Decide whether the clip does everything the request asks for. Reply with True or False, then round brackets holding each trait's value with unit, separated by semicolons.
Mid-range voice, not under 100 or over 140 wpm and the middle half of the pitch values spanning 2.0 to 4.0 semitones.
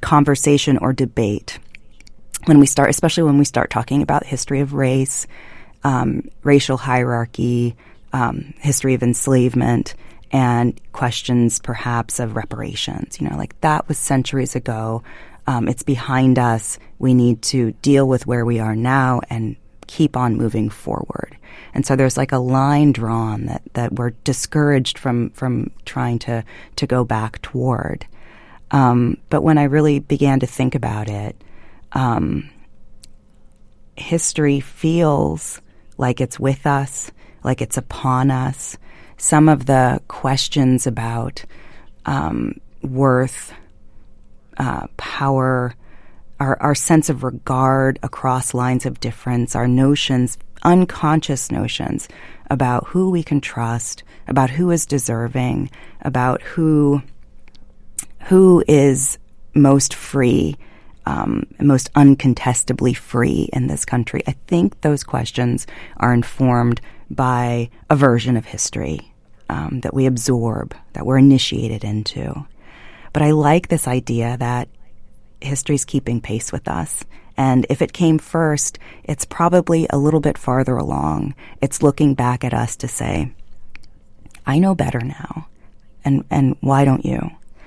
False (130 Hz; 135 wpm; 2.9 semitones)